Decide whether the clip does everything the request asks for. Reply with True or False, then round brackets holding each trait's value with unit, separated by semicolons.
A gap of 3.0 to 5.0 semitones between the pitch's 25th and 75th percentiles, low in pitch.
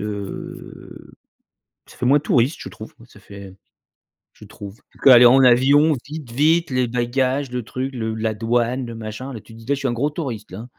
True (3.3 semitones; 125 Hz)